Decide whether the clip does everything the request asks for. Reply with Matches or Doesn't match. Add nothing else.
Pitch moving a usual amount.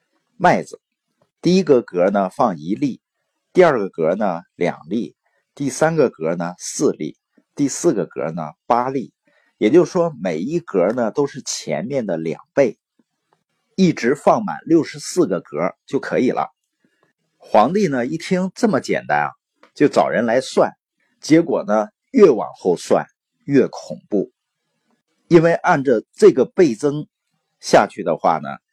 Doesn't match